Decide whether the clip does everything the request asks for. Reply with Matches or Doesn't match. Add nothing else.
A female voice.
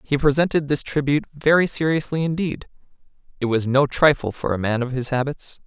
Doesn't match